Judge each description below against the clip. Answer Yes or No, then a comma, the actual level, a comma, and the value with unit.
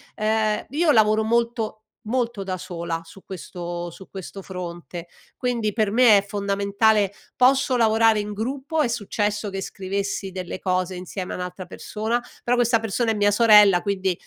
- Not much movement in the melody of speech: No, average, 3.2 semitones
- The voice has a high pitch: Yes, high, 210 Hz